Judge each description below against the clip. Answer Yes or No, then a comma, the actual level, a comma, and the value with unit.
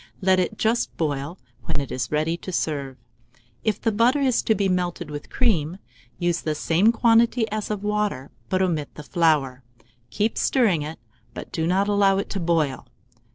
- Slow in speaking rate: No, average, 180 wpm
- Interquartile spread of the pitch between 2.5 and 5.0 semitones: No, wide, 5.5 semitones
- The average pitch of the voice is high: No, medium, 180 Hz